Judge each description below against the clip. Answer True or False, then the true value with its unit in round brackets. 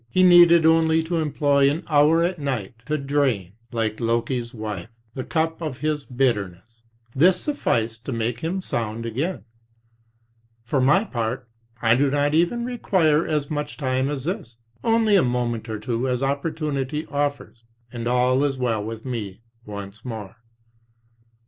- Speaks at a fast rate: False (155 wpm)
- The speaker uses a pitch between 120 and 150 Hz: True (135 Hz)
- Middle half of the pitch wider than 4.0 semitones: True (5.3 semitones)